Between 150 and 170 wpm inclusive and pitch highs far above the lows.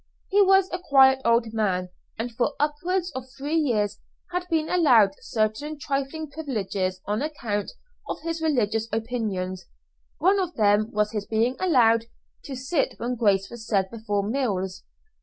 Yes: average, 155 wpm; wide, 6.1 semitones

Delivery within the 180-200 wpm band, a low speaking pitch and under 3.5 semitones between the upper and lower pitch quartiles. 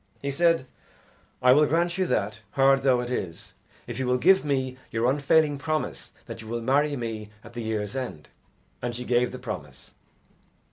No: average, 185 wpm; low, 130 Hz; average, 3.8 semitones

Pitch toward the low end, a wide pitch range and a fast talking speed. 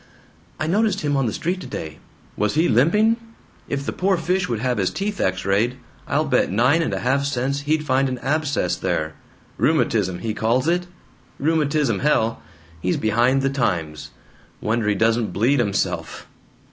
No: low, 130 Hz; wide, 5.9 semitones; average, 170 wpm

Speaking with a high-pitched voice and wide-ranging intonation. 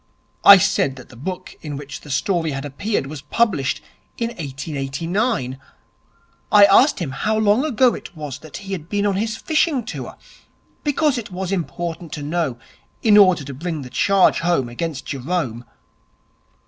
No: medium, 170 Hz; wide, 6.6 semitones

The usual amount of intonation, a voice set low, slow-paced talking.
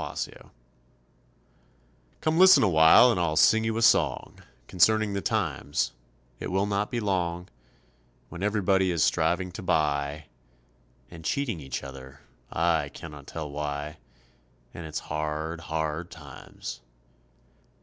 Yes: average, 4.5 semitones; very low, 85 Hz; slow, 130 wpm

